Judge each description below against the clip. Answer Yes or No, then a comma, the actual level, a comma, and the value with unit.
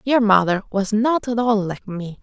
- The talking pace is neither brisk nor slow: No, fast, 215 wpm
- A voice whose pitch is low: No, high, 215 Hz